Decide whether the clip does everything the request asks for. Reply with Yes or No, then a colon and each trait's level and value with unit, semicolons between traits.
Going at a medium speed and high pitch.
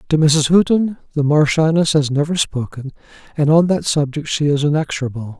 No: average, 165 wpm; medium, 150 Hz